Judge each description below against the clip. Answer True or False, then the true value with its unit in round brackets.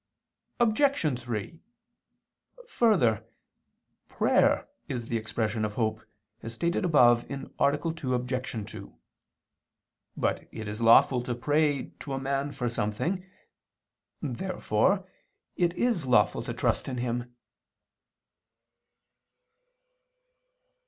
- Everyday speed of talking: False (100 wpm)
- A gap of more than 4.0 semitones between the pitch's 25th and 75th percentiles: True (5.4 semitones)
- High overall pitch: False (125 Hz)